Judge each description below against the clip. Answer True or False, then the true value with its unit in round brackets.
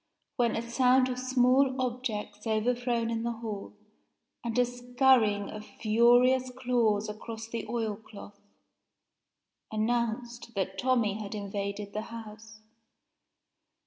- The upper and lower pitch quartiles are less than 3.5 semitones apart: True (2.5 semitones)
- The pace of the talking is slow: True (115 wpm)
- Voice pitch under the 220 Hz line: False (230 Hz)